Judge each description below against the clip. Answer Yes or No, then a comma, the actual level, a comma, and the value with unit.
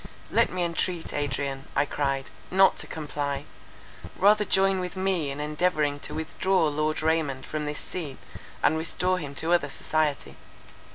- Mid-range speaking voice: Yes, medium, 155 Hz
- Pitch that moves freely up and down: No, average, 3.9 semitones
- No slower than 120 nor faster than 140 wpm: No, average, 155 wpm